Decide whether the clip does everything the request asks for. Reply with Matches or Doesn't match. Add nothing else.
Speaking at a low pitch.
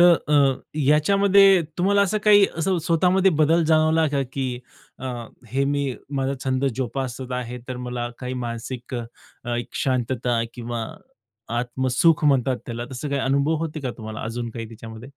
Matches